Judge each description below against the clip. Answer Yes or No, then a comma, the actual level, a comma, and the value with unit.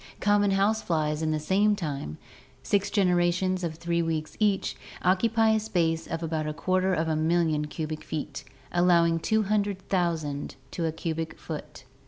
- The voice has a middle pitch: Yes, medium, 170 Hz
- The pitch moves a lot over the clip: No, average, 3.7 semitones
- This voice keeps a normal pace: Yes, average, 170 wpm